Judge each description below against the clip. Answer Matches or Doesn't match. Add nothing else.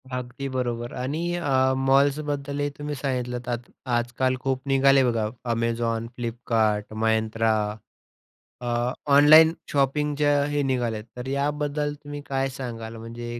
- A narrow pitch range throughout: Doesn't match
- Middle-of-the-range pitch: Doesn't match